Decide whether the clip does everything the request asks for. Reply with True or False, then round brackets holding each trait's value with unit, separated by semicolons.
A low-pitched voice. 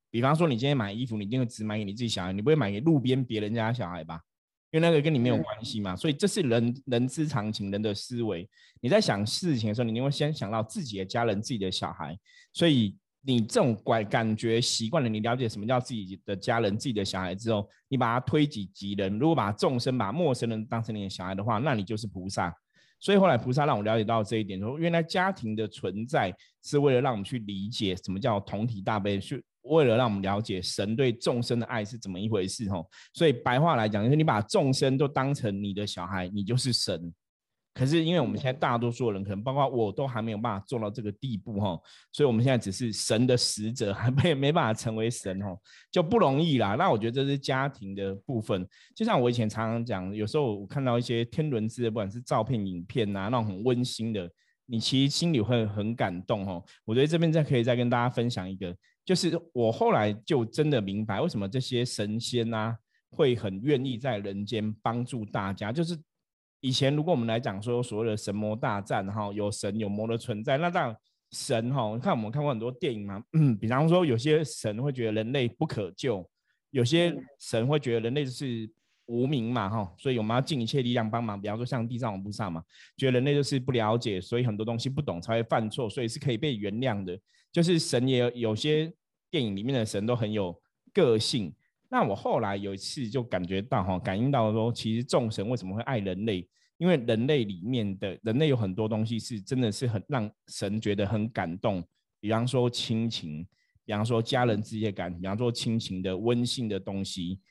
True (115 Hz)